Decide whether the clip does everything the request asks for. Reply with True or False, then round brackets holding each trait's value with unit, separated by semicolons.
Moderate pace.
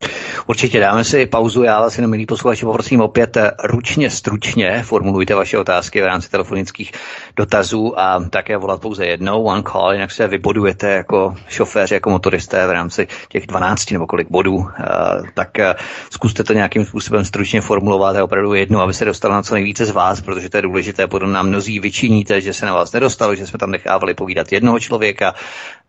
False (185 wpm)